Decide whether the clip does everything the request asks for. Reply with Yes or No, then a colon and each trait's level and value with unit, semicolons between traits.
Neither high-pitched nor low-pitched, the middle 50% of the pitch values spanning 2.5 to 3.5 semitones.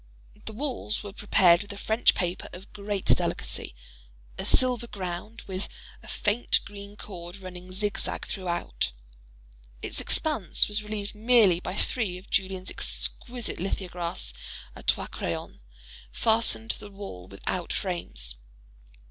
No: high, 200 Hz; average, 3.0 semitones